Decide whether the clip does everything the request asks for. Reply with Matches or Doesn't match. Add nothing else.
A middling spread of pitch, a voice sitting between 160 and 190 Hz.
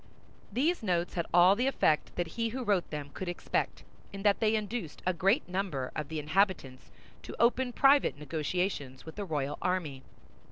Doesn't match